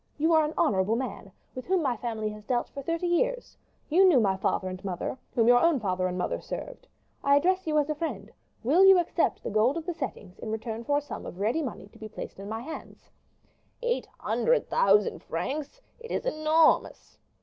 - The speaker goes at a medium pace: No, fast, 215 wpm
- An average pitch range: No, wide, 7.4 semitones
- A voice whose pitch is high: Yes, very high, 270 Hz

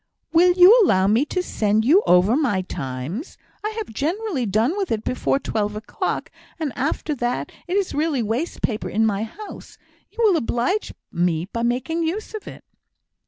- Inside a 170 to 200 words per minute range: Yes, average, 175 wpm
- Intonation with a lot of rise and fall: Yes, wide, 8.8 semitones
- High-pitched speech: Yes, very high, 255 Hz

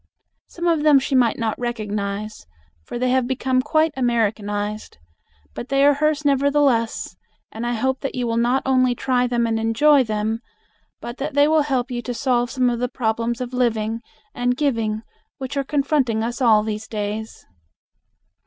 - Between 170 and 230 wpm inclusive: Yes, average, 175 wpm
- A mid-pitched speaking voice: No, high, 245 Hz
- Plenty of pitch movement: No, average, 3.2 semitones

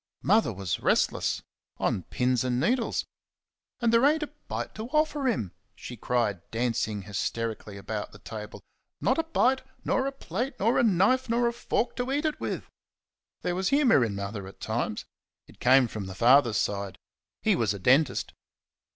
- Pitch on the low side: Yes, low, 130 Hz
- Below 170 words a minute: No, average, 175 wpm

